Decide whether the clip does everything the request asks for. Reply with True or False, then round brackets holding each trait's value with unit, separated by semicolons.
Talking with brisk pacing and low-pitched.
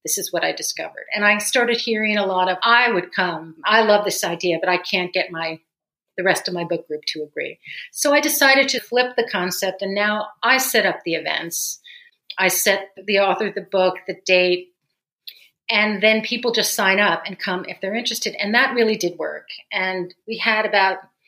False (210 wpm; 195 Hz)